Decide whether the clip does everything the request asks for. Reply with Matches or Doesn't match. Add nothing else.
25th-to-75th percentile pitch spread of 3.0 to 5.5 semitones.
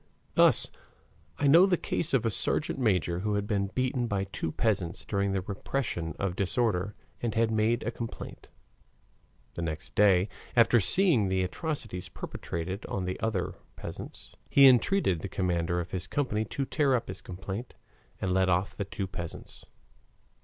Matches